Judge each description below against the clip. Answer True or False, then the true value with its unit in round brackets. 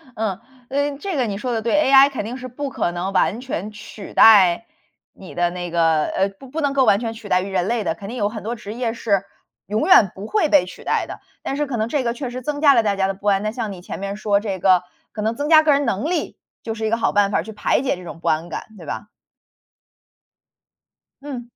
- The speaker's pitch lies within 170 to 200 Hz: False (220 Hz)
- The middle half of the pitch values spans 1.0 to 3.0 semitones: False (4.7 semitones)